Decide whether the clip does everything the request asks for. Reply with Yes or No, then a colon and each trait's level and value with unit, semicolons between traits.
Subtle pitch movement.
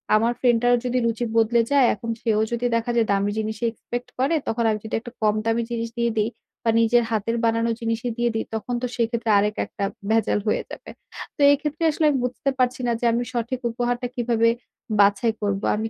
Yes: narrow, 1.6 semitones